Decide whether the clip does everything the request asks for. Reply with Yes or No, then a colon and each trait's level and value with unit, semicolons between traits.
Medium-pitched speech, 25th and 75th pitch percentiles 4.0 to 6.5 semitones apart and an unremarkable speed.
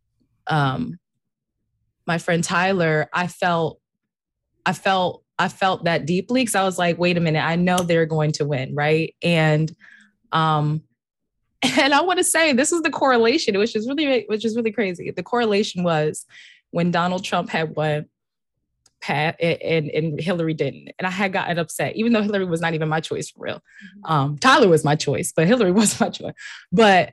Yes: medium, 175 Hz; average, 5.0 semitones; average, 185 wpm